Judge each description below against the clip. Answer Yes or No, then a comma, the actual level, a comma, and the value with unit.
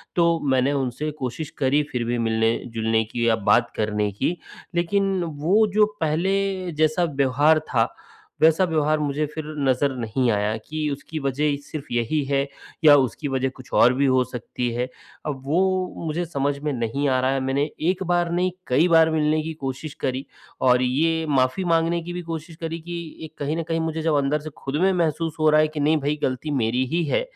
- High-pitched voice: No, medium, 150 Hz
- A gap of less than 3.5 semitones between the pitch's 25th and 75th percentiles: No, average, 4.0 semitones